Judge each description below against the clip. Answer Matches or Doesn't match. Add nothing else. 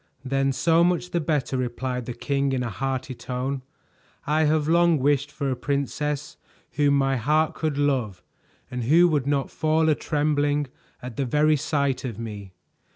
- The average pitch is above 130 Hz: Matches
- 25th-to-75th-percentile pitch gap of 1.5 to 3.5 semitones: Matches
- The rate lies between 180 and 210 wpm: Doesn't match